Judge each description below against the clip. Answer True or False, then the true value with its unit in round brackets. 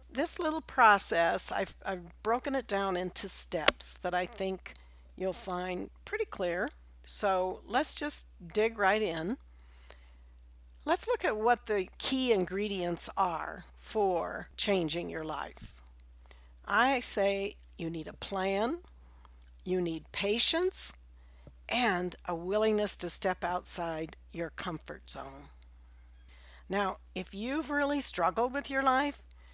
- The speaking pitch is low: False (180 Hz)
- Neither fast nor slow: False (125 wpm)